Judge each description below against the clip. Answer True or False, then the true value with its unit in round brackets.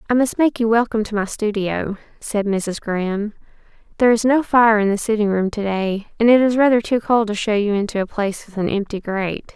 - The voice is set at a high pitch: True (215 Hz)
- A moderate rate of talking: False (230 wpm)